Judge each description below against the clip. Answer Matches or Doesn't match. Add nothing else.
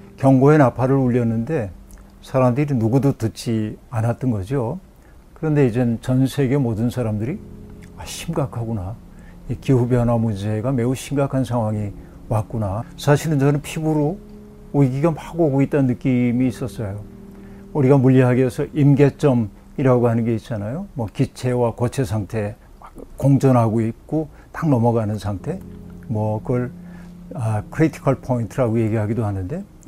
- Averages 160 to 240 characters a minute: Doesn't match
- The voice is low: Matches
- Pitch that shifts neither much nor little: Matches